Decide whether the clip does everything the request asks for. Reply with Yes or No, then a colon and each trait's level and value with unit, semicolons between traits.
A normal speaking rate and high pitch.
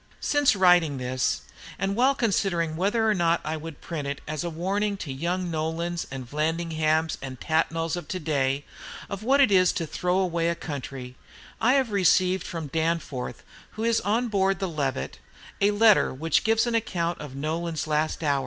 No: average, 185 wpm; medium, 170 Hz